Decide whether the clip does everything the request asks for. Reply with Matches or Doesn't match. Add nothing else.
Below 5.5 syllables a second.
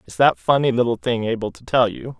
Doesn't match